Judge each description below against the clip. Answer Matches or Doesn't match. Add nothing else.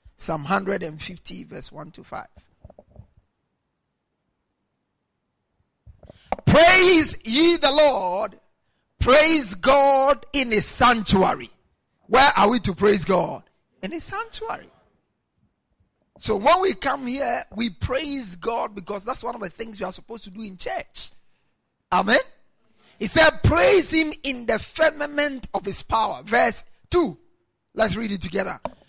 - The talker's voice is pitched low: Doesn't match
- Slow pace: Matches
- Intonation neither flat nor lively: Doesn't match